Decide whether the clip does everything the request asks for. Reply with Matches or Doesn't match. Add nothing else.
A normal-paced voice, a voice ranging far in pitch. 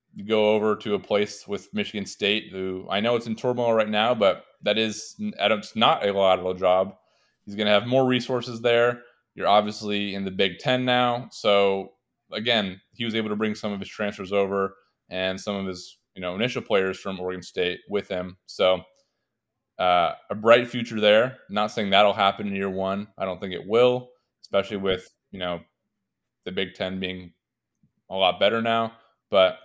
Doesn't match